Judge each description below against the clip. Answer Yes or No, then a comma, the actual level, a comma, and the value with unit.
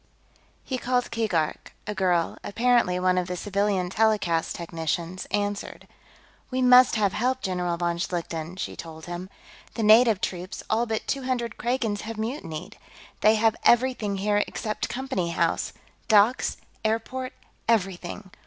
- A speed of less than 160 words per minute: Yes, average, 140 wpm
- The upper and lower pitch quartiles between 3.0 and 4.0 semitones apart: No, average, 4.4 semitones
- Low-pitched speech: No, high, 205 Hz